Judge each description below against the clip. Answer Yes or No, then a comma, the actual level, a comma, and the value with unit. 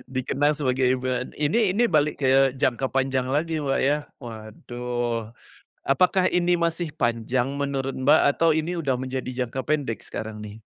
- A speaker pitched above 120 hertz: Yes, low, 135 Hz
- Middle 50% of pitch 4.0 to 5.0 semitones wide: No, average, 3.4 semitones